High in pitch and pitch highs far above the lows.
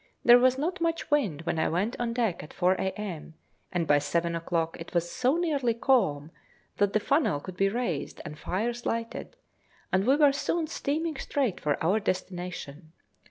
Yes: high, 200 Hz; wide, 7.6 semitones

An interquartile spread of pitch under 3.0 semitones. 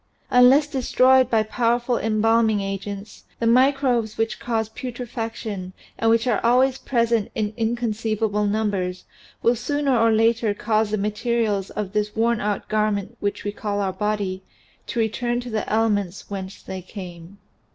Yes: narrow, 2.4 semitones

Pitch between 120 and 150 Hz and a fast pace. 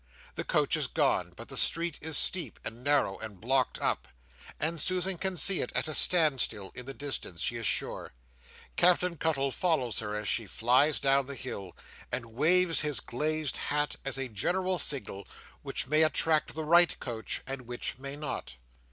No: medium, 140 Hz; average, 185 wpm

